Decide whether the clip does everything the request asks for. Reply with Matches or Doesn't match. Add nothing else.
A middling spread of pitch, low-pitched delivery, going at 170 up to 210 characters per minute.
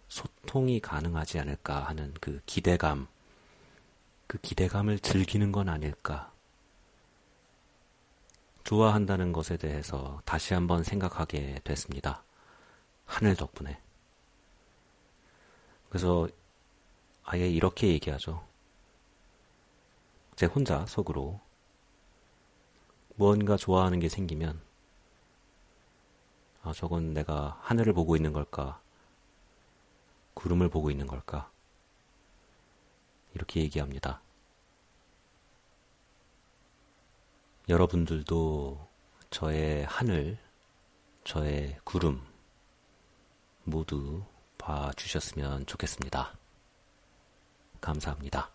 Matches